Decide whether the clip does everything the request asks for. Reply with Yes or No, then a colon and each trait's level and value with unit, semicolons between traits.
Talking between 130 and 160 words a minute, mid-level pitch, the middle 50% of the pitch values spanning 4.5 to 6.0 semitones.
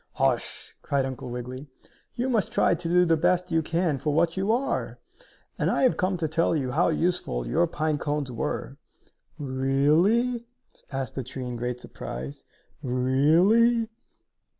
Yes: average, 155 wpm; medium, 155 Hz; wide, 5.4 semitones